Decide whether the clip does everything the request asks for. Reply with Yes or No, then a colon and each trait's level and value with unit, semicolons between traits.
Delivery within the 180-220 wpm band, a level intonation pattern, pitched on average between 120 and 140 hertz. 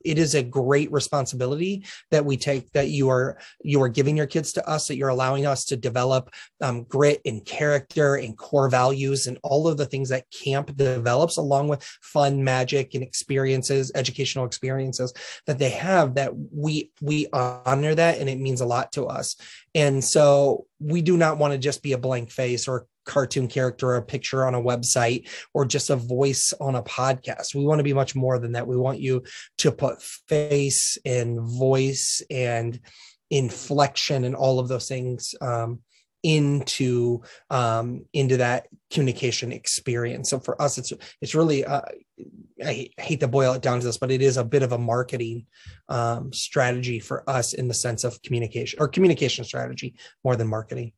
Yes: average, 185 wpm; narrow, 2.2 semitones; low, 135 Hz